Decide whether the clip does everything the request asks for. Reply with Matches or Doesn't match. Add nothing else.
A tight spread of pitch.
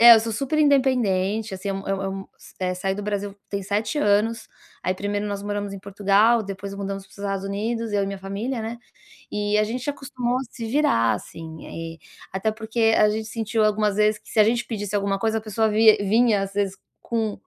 Matches